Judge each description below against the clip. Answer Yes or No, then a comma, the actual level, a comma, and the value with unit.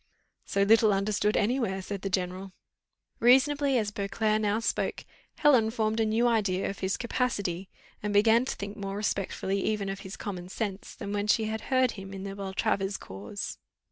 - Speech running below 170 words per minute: No, average, 180 wpm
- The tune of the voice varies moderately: No, narrow, 2.3 semitones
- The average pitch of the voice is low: No, high, 205 Hz